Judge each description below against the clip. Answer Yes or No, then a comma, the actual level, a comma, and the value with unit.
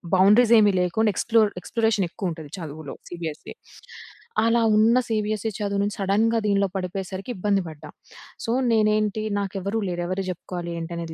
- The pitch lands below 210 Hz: Yes, high, 200 Hz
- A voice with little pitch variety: No, average, 3.3 semitones